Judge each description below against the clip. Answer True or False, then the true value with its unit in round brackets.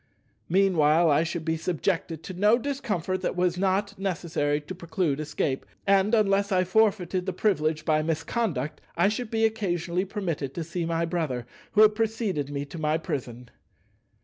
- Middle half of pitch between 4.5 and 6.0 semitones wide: False (4.1 semitones)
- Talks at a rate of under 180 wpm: True (165 wpm)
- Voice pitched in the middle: True (175 Hz)